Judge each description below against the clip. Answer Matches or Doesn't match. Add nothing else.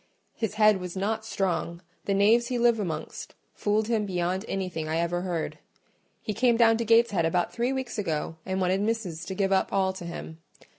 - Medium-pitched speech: Doesn't match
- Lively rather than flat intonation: Doesn't match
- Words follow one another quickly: Doesn't match